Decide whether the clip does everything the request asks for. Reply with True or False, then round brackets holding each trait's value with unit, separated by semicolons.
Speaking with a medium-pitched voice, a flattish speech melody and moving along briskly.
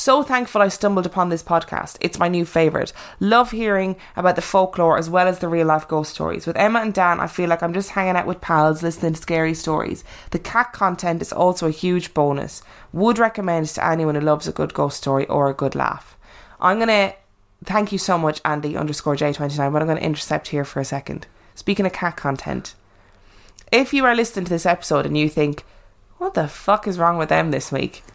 False (170 Hz; 4.1 semitones; 220 wpm)